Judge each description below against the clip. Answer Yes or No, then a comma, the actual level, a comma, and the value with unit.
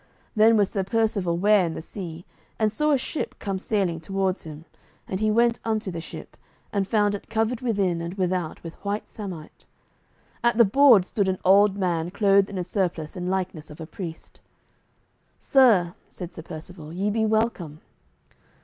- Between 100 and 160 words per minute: No, average, 175 wpm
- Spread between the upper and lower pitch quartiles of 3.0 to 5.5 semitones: Yes, average, 3.7 semitones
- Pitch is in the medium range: No, high, 195 Hz